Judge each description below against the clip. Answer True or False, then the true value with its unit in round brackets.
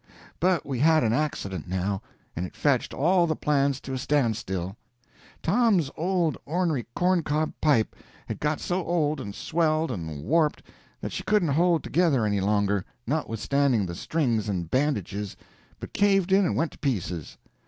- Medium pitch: True (145 Hz)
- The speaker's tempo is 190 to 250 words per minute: False (165 wpm)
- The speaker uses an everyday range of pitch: False (8.0 semitones)